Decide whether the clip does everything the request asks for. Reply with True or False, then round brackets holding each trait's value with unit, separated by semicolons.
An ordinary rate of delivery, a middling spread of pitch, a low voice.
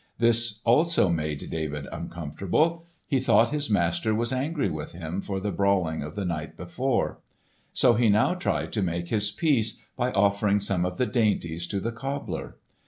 False (170 wpm; 5.9 semitones; 105 Hz)